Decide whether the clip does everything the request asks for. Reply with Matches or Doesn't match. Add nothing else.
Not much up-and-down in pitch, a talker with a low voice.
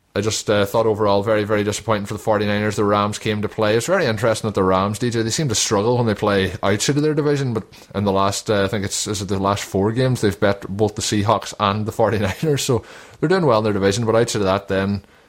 Matches